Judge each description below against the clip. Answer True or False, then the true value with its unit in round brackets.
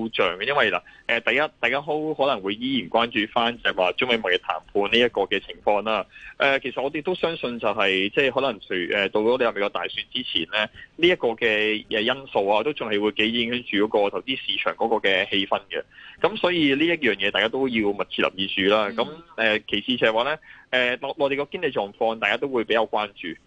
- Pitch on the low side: True (120 Hz)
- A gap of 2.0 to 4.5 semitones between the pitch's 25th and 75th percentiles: False (5.0 semitones)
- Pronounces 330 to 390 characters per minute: True (345 characters per minute)